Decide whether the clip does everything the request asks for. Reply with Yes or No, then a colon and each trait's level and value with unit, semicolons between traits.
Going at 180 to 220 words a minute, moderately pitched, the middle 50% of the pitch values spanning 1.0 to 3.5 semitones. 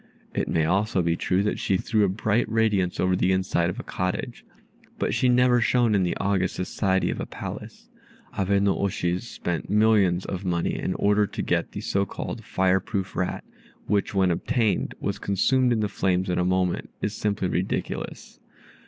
No: average, 190 wpm; very low, 95 Hz; narrow, 2.5 semitones